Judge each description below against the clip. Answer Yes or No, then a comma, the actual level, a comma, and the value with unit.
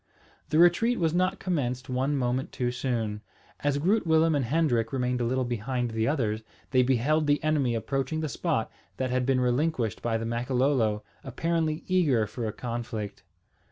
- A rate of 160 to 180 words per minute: Yes, average, 170 wpm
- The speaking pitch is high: No, low, 130 Hz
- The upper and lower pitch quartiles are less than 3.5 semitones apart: No, average, 4.5 semitones